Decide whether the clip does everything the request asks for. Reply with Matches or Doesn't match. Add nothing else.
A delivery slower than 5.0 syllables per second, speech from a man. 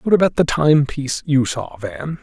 Matches